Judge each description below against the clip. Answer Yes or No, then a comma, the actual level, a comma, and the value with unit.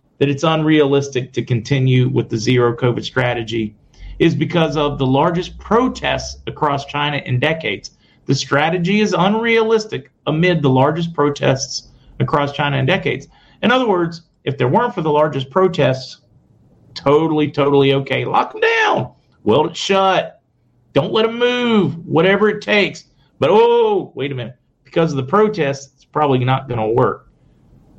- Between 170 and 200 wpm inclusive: No, average, 155 wpm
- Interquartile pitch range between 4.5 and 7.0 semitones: Yes, average, 5.3 semitones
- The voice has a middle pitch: Yes, medium, 145 Hz